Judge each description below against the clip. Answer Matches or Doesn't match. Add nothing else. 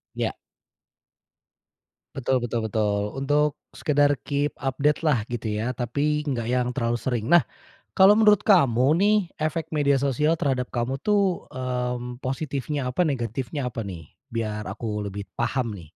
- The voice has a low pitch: Matches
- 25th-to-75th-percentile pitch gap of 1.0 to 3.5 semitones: Doesn't match